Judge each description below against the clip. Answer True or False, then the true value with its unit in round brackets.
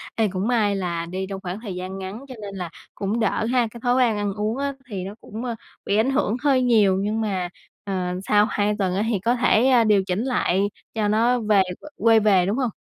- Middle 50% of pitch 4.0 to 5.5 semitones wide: False (3.4 semitones)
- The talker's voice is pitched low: False (210 Hz)